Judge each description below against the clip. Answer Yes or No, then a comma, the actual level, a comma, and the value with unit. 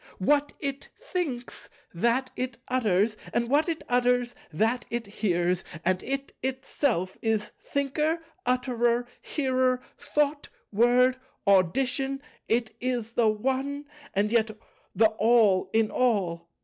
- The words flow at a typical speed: No, slow, 120 wpm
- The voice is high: Yes, high, 240 Hz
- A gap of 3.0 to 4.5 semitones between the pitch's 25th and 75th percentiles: Yes, average, 3.6 semitones